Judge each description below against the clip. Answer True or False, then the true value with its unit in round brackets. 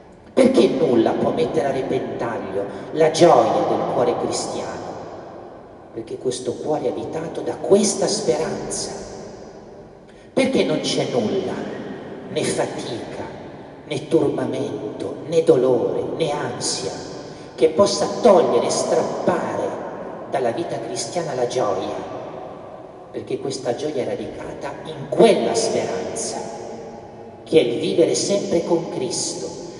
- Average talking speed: False (110 wpm)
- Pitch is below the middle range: False (170 Hz)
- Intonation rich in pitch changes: False (4.2 semitones)